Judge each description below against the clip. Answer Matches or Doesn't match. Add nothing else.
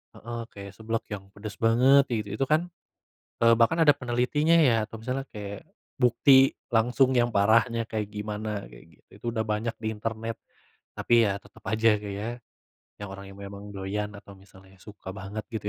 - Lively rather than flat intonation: Doesn't match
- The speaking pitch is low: Matches